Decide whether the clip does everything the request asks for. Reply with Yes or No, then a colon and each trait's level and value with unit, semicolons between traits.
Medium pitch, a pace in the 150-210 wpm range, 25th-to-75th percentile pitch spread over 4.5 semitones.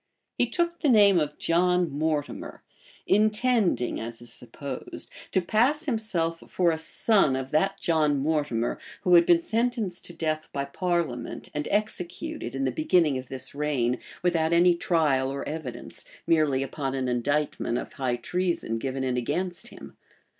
Yes: medium, 160 Hz; average, 160 wpm; average, 5.1 semitones